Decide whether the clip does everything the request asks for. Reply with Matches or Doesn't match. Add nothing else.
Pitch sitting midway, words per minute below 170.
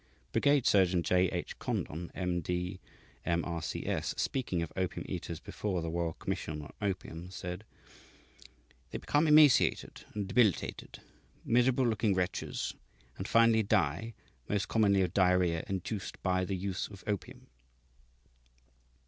Doesn't match